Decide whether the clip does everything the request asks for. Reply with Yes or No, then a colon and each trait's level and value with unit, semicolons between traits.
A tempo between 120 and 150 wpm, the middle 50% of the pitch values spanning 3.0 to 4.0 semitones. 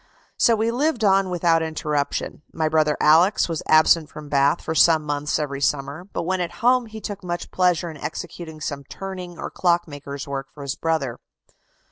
No: average, 180 wpm; average, 3.7 semitones